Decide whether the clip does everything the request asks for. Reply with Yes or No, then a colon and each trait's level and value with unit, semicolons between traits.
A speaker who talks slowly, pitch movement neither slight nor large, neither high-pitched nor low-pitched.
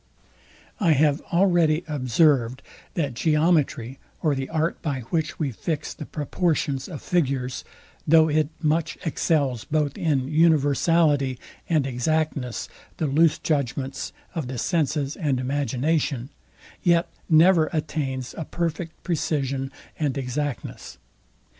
Yes: slow, 115 wpm; average, 3.2 semitones; medium, 150 Hz